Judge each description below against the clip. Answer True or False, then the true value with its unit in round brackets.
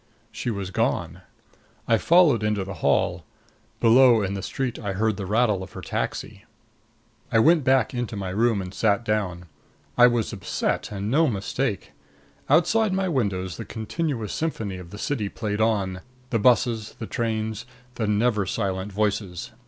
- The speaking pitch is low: True (110 Hz)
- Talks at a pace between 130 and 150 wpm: False (160 wpm)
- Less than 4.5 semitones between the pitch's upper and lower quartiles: True (3.7 semitones)